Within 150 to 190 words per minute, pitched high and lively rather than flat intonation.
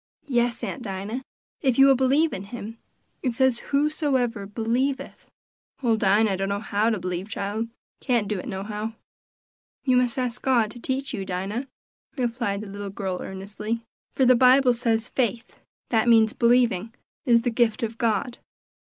No: average, 160 wpm; high, 230 Hz; average, 3.5 semitones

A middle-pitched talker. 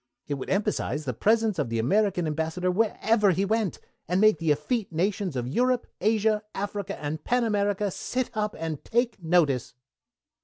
No: high, 195 Hz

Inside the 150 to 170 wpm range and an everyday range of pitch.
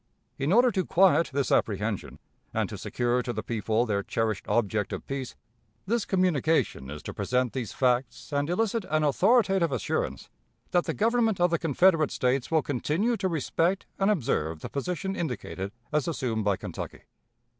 No: average, 165 wpm; wide, 7.6 semitones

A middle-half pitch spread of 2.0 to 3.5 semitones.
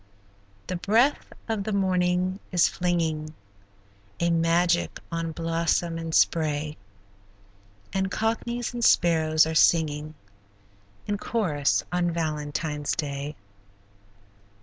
Yes: average, 3.1 semitones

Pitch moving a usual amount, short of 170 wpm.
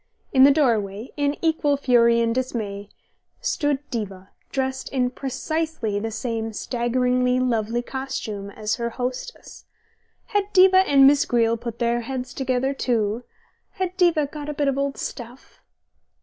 Yes: average, 3.4 semitones; average, 145 wpm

